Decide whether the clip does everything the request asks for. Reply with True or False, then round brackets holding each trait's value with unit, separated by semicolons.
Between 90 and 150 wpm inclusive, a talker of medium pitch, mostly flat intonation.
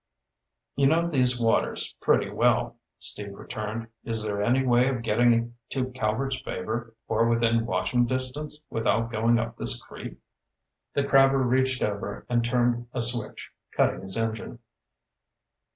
False (140 wpm; 120 Hz; 2.3 semitones)